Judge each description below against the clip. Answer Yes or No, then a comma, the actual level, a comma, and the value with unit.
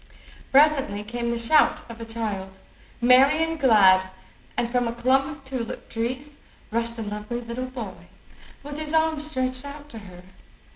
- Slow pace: No, average, 160 wpm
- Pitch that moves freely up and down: No, average, 3.8 semitones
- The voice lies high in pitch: Yes, high, 245 Hz